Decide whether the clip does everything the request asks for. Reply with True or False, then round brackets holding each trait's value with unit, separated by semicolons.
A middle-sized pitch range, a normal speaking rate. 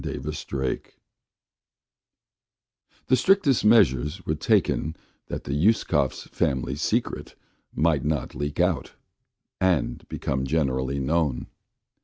False (4.3 semitones; 100 wpm)